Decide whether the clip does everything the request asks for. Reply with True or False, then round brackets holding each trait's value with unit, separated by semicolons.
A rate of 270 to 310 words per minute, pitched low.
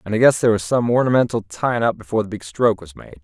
True (280 wpm; 110 Hz)